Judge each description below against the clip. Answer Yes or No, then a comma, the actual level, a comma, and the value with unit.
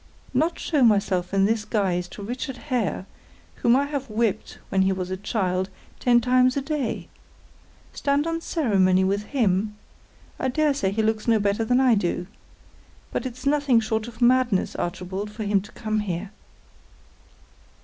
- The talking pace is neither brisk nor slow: Yes, average, 165 wpm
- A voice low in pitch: No, high, 220 Hz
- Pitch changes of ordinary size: Yes, average, 4.6 semitones